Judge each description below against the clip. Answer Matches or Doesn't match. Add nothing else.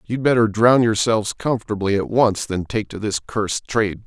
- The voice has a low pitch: Matches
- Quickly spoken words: Doesn't match